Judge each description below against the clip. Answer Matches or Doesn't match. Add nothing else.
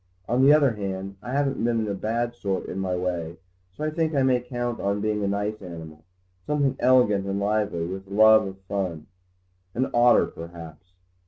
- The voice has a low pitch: Matches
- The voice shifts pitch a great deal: Doesn't match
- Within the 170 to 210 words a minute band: Matches